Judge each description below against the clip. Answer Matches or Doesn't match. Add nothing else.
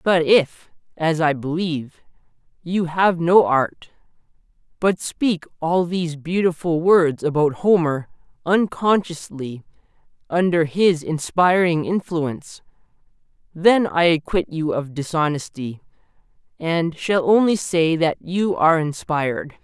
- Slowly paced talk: Matches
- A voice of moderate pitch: Matches